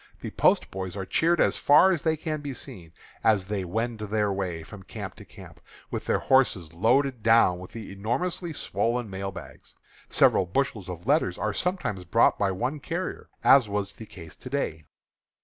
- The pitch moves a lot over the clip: Yes, wide, 6.4 semitones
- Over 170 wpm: Yes, average, 185 wpm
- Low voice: Yes, low, 105 Hz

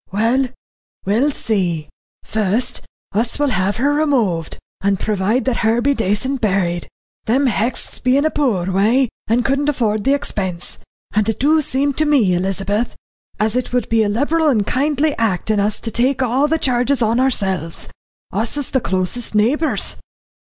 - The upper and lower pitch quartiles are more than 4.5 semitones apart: Yes, average, 5.0 semitones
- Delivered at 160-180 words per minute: Yes, average, 170 wpm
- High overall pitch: Yes, high, 230 Hz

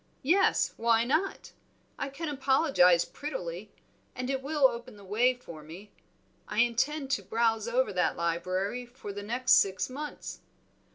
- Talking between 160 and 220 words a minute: No, average, 150 wpm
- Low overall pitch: No, high, 235 Hz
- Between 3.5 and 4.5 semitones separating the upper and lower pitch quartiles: No, average, 5.3 semitones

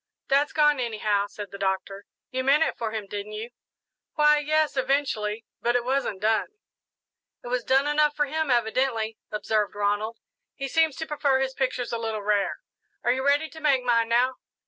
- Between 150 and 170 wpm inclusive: No, average, 185 wpm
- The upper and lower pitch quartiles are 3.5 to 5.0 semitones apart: Yes, average, 4.7 semitones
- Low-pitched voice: No, high, 245 Hz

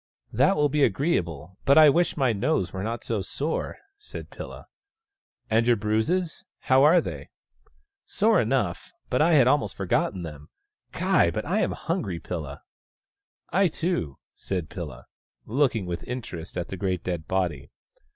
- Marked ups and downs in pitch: Yes, wide, 8.9 semitones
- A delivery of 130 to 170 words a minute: No, average, 180 wpm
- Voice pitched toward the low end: Yes, low, 110 Hz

